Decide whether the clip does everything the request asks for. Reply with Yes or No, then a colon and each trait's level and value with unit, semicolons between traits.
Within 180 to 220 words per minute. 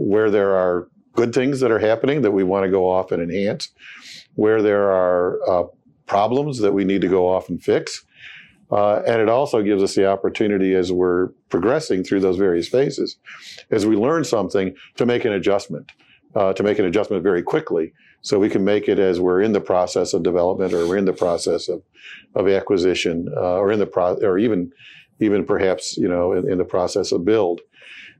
Yes: fast, 205 wpm